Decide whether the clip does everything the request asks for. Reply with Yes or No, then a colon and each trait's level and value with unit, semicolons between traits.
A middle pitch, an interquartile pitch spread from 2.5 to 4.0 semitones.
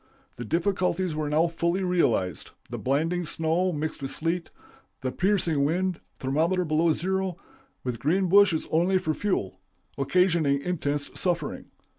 Yes: medium, 165 Hz; average, 3.7 semitones